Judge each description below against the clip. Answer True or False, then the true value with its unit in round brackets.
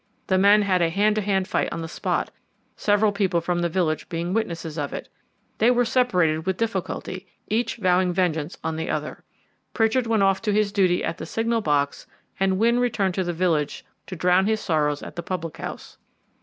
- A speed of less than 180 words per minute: False (200 wpm)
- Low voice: False (185 Hz)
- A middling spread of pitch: True (3.9 semitones)